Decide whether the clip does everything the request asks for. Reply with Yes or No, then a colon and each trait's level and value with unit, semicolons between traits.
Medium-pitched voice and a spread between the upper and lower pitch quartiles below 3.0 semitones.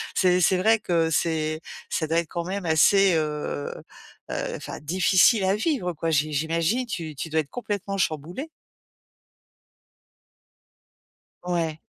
No: medium, 170 Hz; average, 3.5 semitones